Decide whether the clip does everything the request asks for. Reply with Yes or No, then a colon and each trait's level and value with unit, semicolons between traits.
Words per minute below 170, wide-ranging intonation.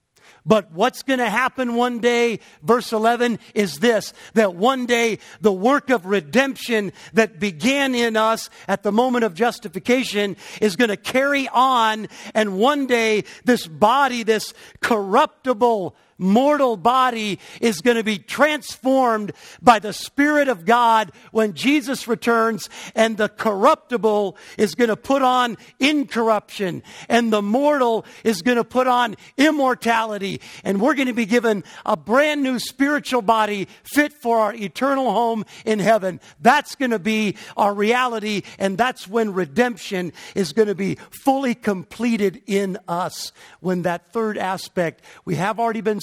No: average, 150 wpm; average, 3.2 semitones